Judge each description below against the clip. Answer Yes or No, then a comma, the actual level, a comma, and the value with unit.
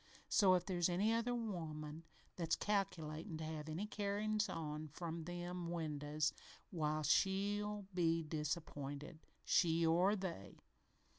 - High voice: No, medium, 170 Hz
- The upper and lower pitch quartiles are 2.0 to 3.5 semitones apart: No, average, 4.0 semitones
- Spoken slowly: Yes, slow, 125 wpm